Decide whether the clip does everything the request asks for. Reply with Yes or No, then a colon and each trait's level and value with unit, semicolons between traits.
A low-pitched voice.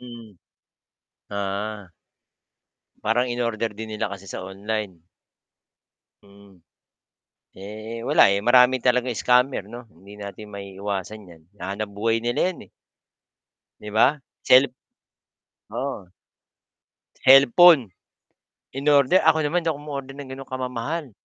Yes: low, 115 Hz